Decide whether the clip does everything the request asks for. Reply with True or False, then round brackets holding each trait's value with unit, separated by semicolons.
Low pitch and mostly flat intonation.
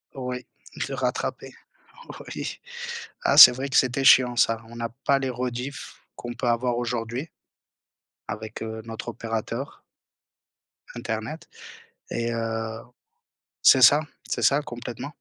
True (120 Hz; 2.2 semitones)